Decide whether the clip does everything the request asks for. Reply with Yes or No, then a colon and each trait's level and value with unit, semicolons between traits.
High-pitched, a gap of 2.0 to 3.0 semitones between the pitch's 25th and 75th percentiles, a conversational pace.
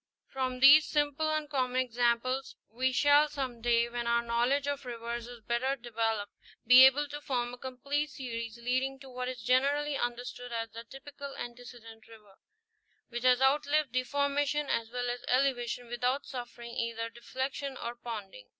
Yes: very high, 250 Hz; average, 2.7 semitones; average, 165 wpm